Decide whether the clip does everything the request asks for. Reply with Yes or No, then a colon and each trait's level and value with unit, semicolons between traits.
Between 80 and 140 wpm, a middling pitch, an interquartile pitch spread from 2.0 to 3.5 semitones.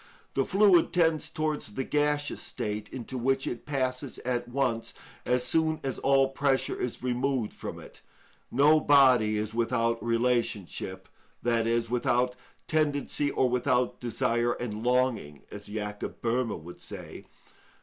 No: slow, 135 wpm; low, 125 Hz; average, 3.1 semitones